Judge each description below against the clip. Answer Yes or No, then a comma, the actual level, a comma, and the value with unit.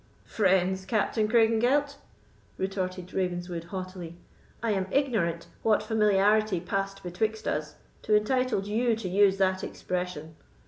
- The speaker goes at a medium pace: No, slow, 120 wpm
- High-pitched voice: Yes, high, 195 Hz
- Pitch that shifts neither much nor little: Yes, average, 3.2 semitones